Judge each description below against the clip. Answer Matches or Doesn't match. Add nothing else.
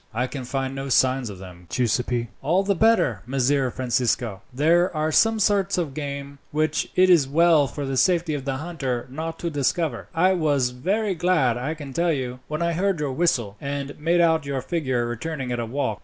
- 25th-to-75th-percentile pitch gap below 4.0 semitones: Doesn't match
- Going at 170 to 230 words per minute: Matches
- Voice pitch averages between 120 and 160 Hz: Matches